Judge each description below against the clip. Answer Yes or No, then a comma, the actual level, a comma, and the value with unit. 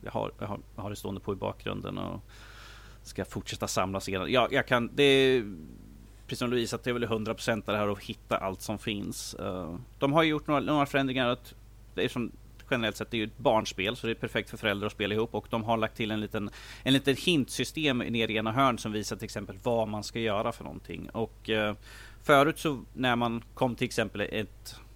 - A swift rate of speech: Yes, fast, 205 wpm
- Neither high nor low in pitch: No, low, 110 Hz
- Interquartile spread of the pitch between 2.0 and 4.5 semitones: Yes, average, 2.8 semitones